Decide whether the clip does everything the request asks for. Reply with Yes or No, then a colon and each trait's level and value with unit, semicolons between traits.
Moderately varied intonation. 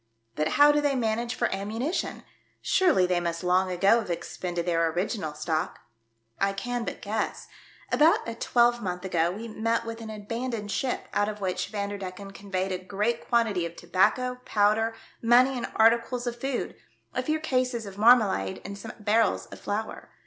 Yes: average, 4.5 semitones